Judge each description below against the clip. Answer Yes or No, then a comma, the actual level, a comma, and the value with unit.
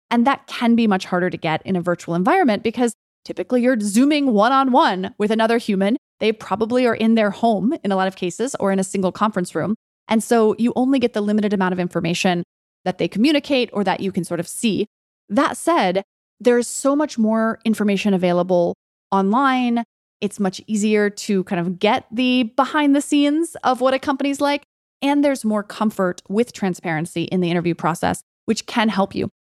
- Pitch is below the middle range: No, high, 215 Hz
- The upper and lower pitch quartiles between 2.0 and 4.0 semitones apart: No, average, 4.9 semitones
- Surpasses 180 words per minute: Yes, average, 200 wpm